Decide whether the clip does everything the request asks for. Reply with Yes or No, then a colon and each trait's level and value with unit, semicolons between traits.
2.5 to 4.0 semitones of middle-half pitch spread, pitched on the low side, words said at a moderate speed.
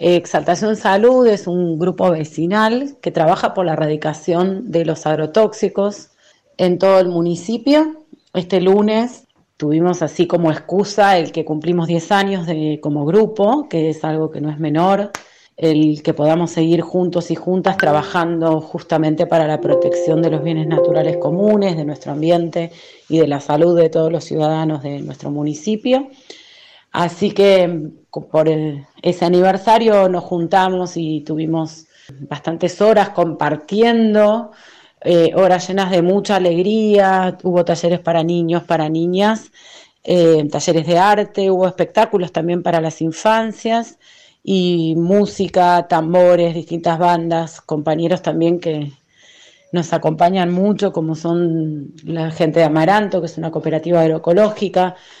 No: average, 3.3 semitones; medium, 175 Hz; average, 140 wpm